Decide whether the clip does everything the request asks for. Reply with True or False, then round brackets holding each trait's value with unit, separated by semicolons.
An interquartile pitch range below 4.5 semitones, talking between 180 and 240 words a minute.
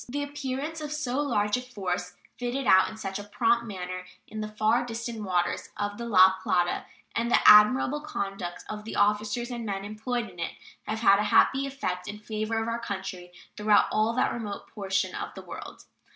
True (3.5 semitones; 195 wpm)